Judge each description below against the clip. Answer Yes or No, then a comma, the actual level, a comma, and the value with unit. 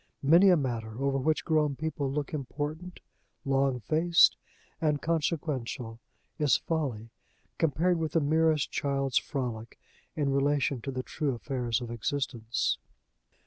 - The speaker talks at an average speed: No, slow, 130 wpm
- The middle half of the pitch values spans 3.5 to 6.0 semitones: Yes, average, 3.8 semitones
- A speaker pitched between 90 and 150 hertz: Yes, medium, 140 Hz